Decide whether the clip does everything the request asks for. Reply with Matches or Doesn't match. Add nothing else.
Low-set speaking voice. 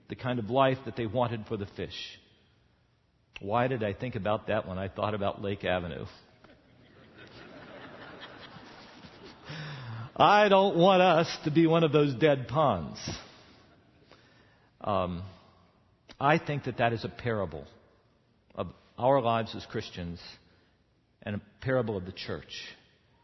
Matches